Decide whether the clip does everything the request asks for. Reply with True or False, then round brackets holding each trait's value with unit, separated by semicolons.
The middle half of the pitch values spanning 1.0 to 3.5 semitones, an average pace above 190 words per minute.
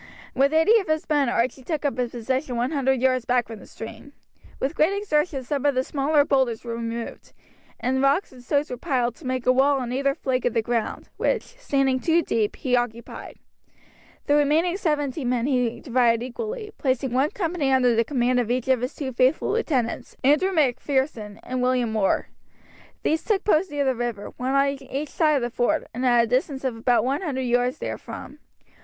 True (3.1 semitones; 200 wpm)